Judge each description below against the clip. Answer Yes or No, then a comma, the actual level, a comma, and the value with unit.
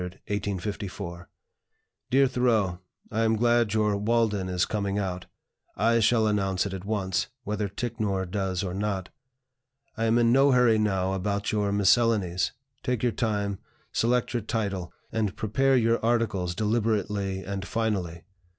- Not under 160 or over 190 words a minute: No, average, 140 wpm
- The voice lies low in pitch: Yes, low, 105 Hz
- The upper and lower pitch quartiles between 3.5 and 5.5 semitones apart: No, average, 3.1 semitones